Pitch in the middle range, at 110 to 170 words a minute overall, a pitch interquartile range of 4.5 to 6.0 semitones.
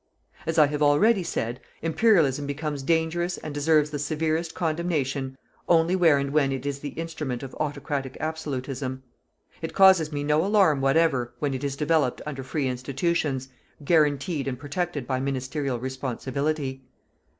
No: medium, 145 Hz; average, 150 wpm; average, 3.1 semitones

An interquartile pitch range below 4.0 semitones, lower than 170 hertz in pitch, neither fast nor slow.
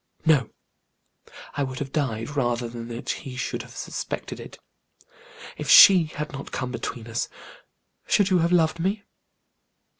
No: average, 5.2 semitones; medium, 140 Hz; average, 150 wpm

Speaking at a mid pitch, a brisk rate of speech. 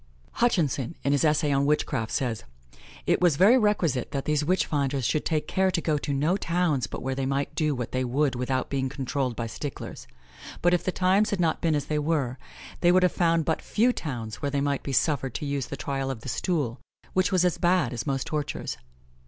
Yes: medium, 145 Hz; fast, 225 wpm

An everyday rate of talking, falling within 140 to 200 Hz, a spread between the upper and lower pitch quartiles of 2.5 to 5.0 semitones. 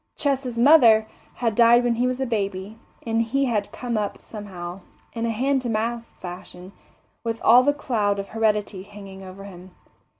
No: average, 175 wpm; high, 225 Hz; average, 3.4 semitones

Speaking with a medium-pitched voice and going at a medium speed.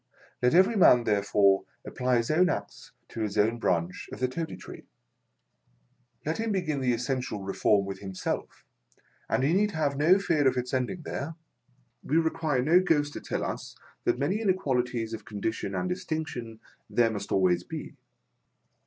No: low, 125 Hz; average, 170 wpm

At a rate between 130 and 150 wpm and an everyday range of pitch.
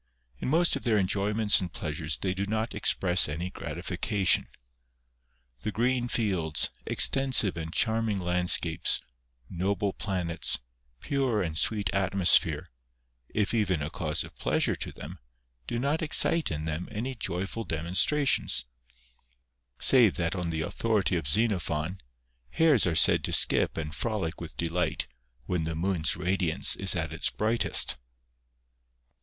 Yes: average, 140 wpm; average, 5.0 semitones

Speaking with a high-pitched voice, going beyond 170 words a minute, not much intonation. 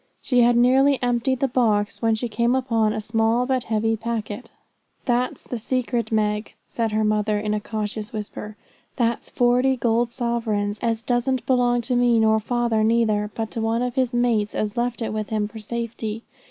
Yes: high, 230 Hz; average, 185 wpm; narrow, 2.0 semitones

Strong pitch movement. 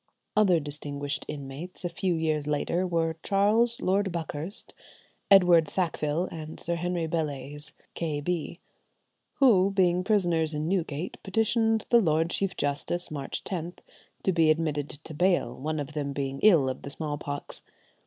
No: average, 3.8 semitones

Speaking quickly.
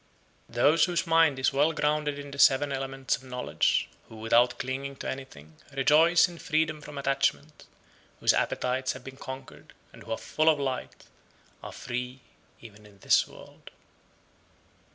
No: average, 160 wpm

